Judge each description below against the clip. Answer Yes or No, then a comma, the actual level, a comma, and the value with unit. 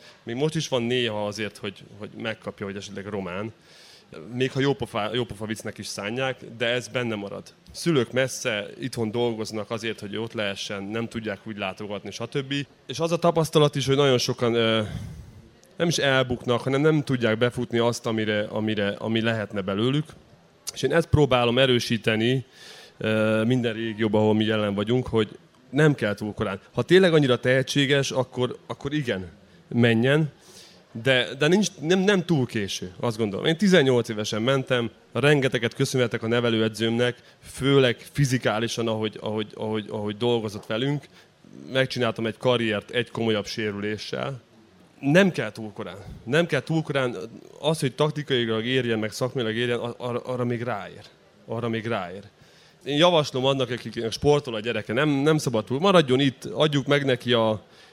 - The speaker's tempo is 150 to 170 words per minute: Yes, fast, 155 wpm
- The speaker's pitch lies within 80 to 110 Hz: No, low, 120 Hz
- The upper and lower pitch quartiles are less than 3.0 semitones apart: No, average, 3.7 semitones